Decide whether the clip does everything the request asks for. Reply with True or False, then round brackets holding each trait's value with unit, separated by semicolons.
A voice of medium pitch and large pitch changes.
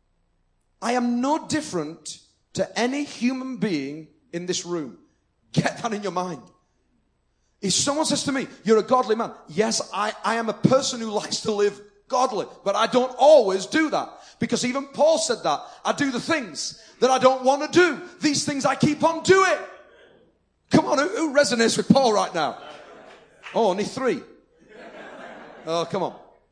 False (235 Hz; 6.6 semitones)